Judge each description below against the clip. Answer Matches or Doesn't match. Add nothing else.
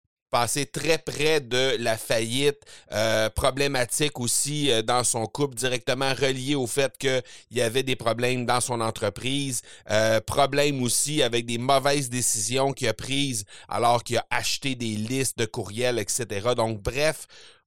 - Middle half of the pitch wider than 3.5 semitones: Doesn't match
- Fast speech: Doesn't match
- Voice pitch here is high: Doesn't match